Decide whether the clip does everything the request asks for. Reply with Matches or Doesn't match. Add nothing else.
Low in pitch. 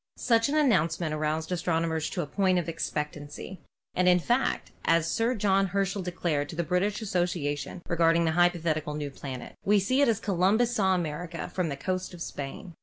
Doesn't match